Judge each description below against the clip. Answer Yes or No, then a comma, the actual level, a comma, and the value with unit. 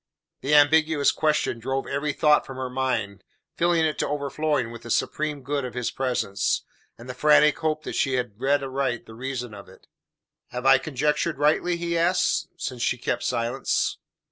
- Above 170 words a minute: Yes, average, 180 wpm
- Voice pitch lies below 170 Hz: Yes, low, 135 Hz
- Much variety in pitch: No, average, 3.4 semitones